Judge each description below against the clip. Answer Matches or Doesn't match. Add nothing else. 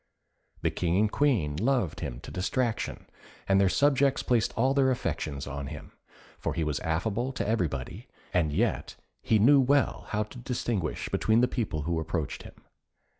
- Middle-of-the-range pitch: Doesn't match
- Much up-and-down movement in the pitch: Matches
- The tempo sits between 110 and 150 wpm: Doesn't match